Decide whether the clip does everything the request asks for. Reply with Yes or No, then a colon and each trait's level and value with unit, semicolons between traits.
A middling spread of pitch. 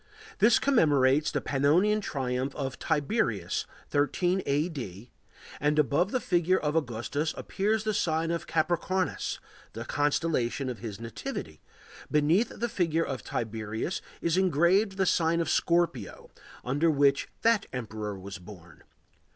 No: wide, 5.7 semitones